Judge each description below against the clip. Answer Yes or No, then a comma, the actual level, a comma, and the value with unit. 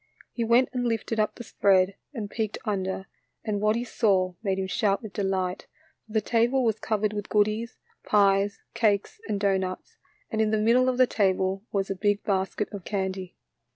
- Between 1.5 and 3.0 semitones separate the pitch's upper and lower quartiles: Yes, narrow, 2.5 semitones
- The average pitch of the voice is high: Yes, high, 205 Hz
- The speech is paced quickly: No, average, 190 wpm